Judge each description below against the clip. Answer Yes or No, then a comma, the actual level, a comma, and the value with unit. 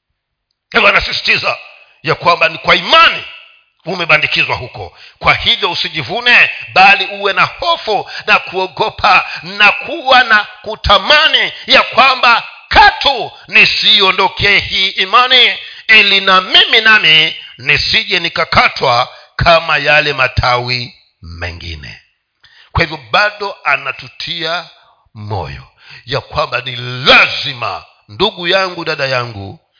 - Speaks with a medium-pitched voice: Yes, medium, 170 Hz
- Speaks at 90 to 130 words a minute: Yes, slow, 100 wpm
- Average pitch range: No, wide, 8.8 semitones